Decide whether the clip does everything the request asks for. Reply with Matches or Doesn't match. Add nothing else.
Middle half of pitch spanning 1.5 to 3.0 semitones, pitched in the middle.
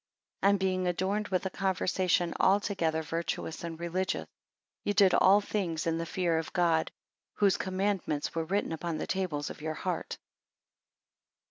Matches